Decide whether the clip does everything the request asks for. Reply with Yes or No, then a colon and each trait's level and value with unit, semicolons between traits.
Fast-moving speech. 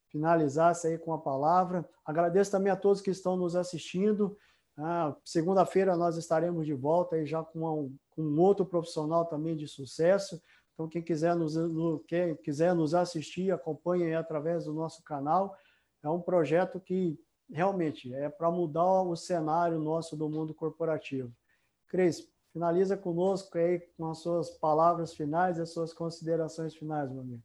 No: average, 160 wpm